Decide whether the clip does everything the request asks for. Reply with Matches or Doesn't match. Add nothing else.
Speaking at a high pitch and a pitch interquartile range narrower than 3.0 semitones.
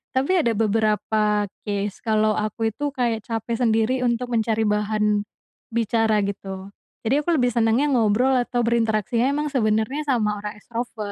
Matches